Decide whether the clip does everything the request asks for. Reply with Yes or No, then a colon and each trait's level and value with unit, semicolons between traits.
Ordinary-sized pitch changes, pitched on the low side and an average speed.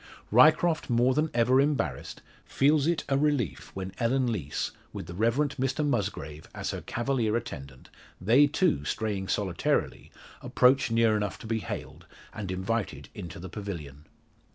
No: wide, 6.3 semitones; low, 115 Hz; average, 150 wpm